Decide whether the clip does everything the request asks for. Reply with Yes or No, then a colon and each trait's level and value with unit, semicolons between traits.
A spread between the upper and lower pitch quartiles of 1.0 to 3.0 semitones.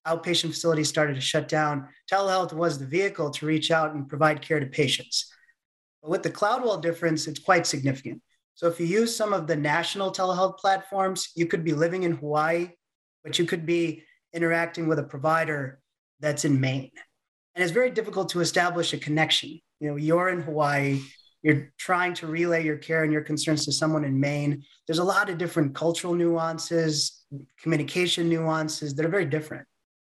Yes: narrow, 2.5 semitones